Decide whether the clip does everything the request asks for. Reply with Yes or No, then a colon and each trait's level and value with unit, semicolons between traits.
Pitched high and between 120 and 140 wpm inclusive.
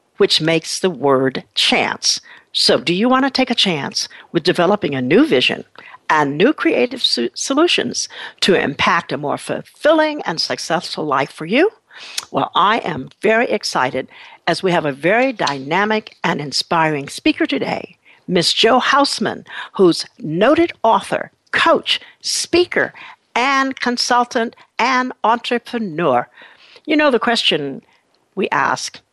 Yes: high, 235 Hz; slow, 135 wpm